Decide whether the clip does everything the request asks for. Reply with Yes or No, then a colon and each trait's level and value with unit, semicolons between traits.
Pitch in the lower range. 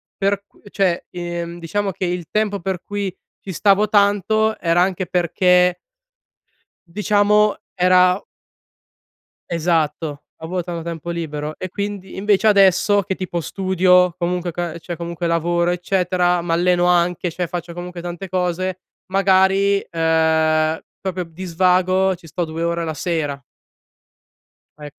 No: medium, 180 Hz